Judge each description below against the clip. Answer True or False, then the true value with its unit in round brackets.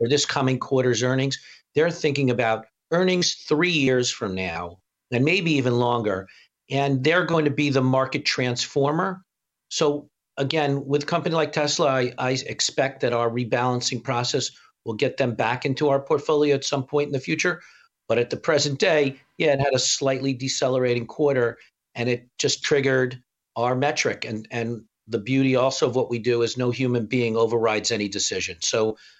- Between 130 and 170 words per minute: False (180 wpm)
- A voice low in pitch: True (130 Hz)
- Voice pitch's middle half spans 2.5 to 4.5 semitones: True (3.1 semitones)